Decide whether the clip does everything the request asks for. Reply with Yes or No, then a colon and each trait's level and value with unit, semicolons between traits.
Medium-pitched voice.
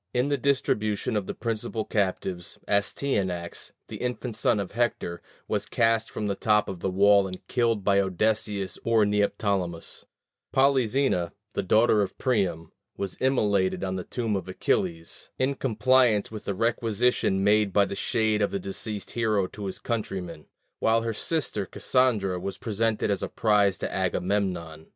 No: low, 105 Hz